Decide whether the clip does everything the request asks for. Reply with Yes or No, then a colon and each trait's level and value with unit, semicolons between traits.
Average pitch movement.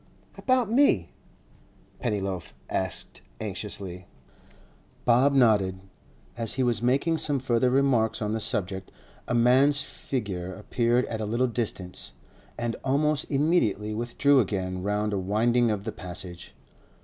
Yes: average, 4.5 semitones